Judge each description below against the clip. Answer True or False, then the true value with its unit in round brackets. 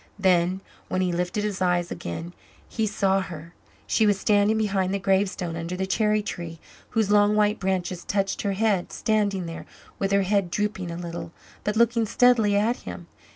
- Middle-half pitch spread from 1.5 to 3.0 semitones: True (2.7 semitones)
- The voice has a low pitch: False (195 Hz)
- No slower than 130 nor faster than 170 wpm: False (180 wpm)